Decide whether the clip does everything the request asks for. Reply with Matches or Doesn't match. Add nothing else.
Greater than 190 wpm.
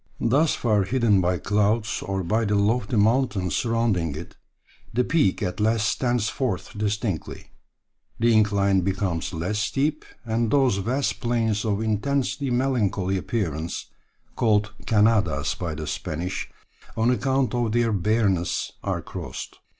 Doesn't match